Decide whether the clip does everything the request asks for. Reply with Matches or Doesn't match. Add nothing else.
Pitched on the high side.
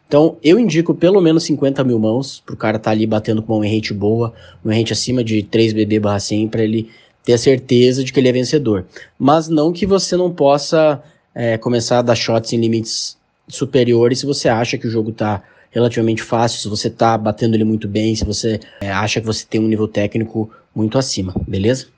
Doesn't match